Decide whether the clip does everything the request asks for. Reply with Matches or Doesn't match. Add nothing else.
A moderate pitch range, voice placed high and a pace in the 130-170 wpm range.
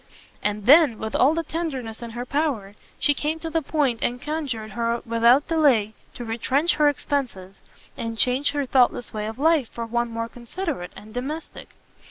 Doesn't match